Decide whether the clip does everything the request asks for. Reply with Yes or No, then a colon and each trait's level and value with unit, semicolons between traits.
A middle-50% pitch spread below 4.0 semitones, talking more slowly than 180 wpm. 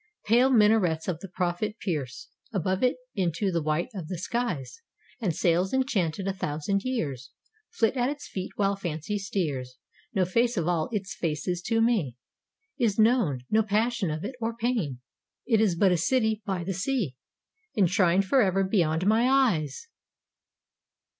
No: average, 5.1 semitones; average, 160 wpm